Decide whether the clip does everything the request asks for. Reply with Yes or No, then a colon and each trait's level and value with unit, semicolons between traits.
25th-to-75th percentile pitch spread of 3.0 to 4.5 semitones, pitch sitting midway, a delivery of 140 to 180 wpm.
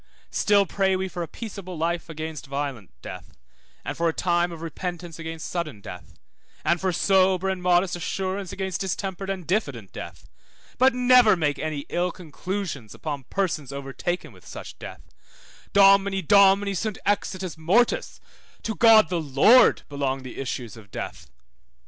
Yes: average, 3.8 semitones; medium, 180 Hz; average, 150 wpm